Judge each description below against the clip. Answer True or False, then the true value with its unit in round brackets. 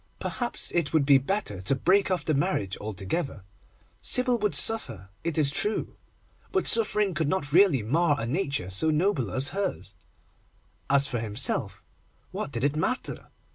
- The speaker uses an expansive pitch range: True (7.7 semitones)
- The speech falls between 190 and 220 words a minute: False (160 wpm)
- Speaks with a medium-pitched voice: True (145 Hz)